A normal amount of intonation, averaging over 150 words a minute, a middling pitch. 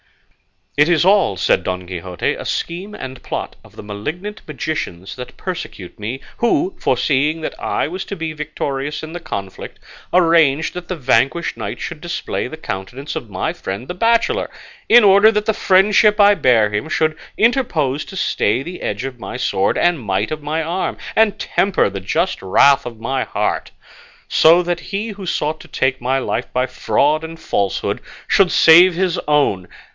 No: wide, 6.5 semitones; average, 180 wpm; medium, 155 Hz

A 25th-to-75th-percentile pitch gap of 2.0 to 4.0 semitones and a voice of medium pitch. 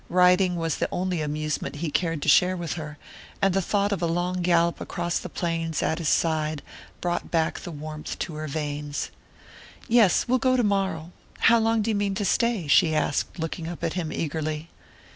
Yes: average, 3.3 semitones; medium, 170 Hz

